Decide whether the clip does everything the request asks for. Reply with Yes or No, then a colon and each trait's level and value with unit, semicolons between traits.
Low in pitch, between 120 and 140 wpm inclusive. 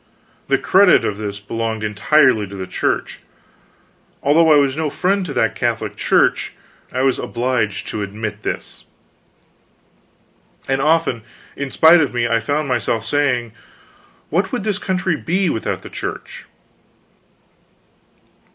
Yes: low, 130 Hz; slow, 135 wpm